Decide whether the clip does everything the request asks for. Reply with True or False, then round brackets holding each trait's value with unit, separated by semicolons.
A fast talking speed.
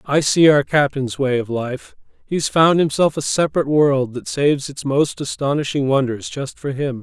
False (190 wpm)